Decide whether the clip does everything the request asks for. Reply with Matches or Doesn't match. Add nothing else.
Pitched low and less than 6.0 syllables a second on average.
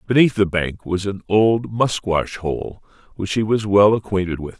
Matches